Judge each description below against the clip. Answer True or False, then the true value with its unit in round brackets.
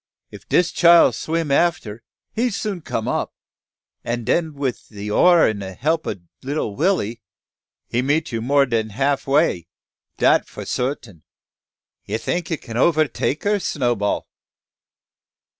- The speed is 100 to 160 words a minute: True (140 wpm)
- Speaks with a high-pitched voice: False (140 Hz)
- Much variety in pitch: True (6.6 semitones)